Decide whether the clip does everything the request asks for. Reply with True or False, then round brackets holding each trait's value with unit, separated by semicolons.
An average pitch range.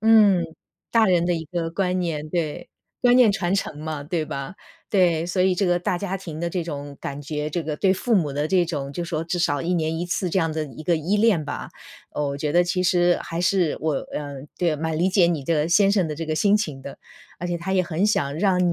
True (3.0 semitones)